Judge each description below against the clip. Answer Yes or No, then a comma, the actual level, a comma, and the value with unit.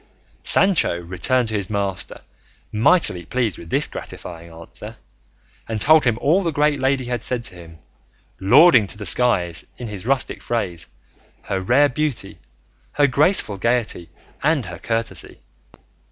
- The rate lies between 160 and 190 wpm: No, average, 145 wpm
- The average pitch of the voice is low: Yes, low, 115 Hz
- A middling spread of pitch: No, wide, 6.5 semitones